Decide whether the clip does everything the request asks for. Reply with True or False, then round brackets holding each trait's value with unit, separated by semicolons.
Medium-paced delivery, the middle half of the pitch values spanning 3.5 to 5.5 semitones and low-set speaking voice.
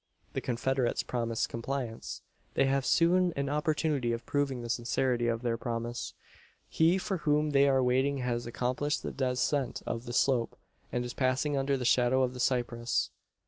False (170 wpm; 2.8 semitones; 130 Hz)